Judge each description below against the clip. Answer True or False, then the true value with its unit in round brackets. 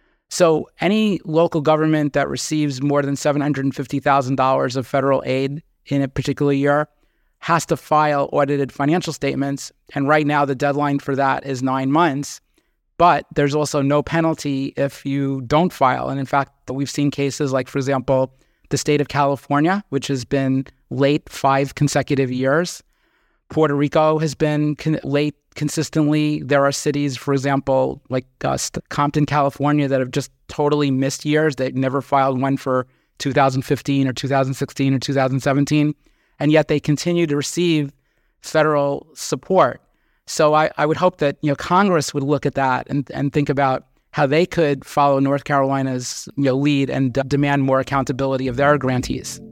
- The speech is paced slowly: False (165 wpm)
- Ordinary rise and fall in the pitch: False (1.6 semitones)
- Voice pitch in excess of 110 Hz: True (140 Hz)